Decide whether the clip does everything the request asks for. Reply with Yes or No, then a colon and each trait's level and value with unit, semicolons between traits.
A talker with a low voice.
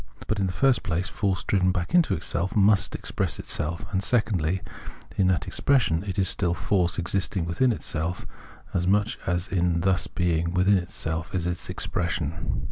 Yes: very low, 90 Hz